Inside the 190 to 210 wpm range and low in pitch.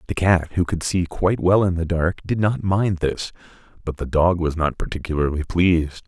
Yes: fast, 205 wpm; very low, 85 Hz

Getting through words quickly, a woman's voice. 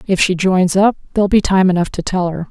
Yes: fast, 265 wpm; female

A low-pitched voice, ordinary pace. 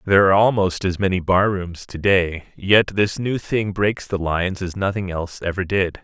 No: very low, 95 Hz; fast, 210 wpm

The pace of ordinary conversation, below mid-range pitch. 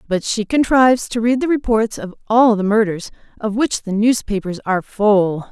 No: average, 185 wpm; high, 220 Hz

